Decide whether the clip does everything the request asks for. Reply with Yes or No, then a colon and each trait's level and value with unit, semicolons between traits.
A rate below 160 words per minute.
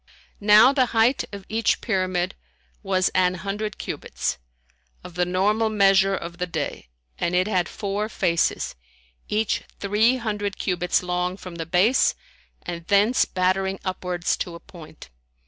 Yes: average, 145 wpm